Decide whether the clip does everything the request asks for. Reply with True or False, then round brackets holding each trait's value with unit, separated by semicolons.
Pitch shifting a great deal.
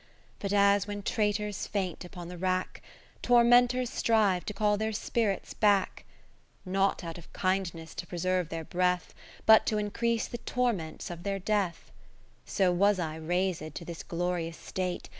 False (3.0 semitones)